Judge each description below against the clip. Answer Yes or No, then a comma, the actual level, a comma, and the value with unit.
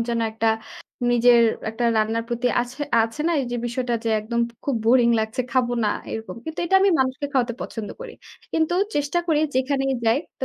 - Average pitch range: Yes, average, 3.2 semitones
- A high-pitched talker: Yes, high, 245 Hz